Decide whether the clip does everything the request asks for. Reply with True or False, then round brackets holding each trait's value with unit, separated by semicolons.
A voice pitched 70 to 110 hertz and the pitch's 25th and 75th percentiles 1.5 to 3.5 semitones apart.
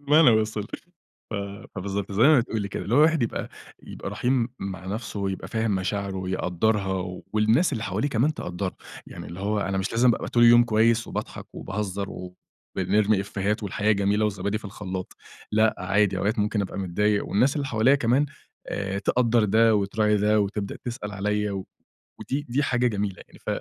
True (105 Hz; 2.8 semitones)